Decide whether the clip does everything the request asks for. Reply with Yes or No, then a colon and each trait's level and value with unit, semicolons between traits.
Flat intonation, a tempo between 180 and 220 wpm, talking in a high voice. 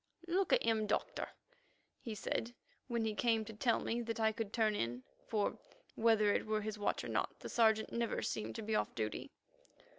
Yes: narrow, 1.4 semitones; average, 200 wpm; high, 220 Hz